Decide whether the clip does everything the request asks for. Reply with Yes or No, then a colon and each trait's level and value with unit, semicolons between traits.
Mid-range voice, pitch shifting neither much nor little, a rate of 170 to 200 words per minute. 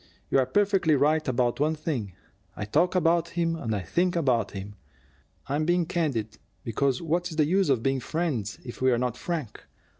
No: medium, 145 Hz; wide, 5.8 semitones; average, 175 wpm